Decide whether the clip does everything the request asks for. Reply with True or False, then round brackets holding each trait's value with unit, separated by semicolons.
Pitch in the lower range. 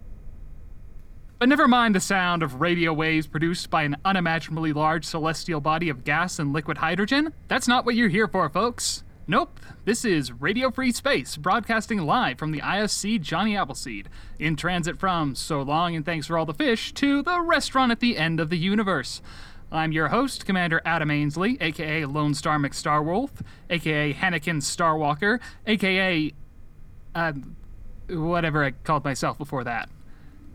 False (165 Hz)